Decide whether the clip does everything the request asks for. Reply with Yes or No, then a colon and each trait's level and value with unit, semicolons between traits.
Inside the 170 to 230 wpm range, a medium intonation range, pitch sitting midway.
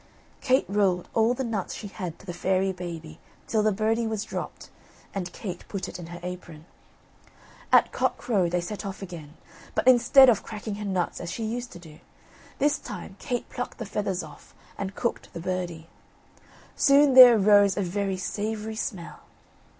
No: average, 175 wpm; average, 3.9 semitones; high, 200 Hz